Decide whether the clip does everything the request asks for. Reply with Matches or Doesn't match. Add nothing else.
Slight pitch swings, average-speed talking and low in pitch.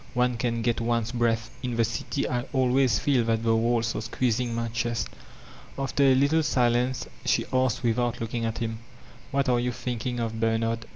Matches